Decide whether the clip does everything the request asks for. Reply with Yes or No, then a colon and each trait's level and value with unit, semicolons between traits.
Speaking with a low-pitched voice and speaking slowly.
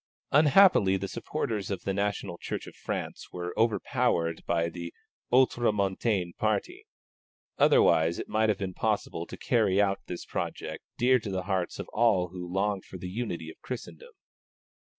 No: low, 100 Hz; average, 155 wpm